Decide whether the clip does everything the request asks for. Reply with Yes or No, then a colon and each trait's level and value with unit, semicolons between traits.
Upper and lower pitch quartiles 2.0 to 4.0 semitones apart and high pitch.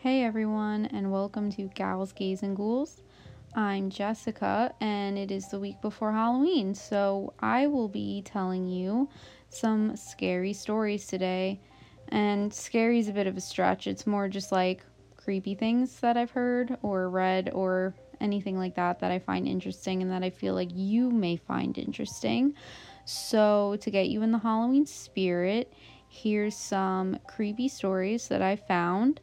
Yes: average, 3.0 semitones; high, 200 Hz